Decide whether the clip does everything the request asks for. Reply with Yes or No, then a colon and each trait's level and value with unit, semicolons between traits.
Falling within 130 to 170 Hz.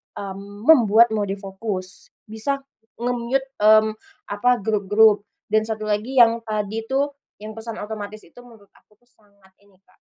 No: high, 215 Hz